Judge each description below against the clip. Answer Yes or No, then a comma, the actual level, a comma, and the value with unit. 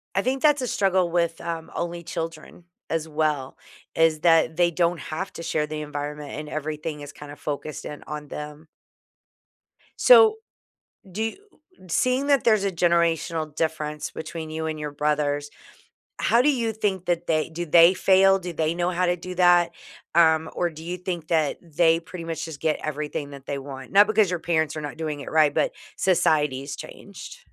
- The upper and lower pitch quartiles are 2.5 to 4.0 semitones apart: Yes, average, 2.8 semitones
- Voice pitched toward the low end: No, medium, 165 Hz